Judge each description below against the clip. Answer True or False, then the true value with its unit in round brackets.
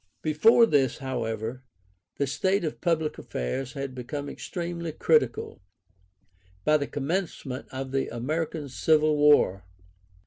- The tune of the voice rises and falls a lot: False (3.4 semitones)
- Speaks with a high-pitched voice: False (145 Hz)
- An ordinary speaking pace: False (115 wpm)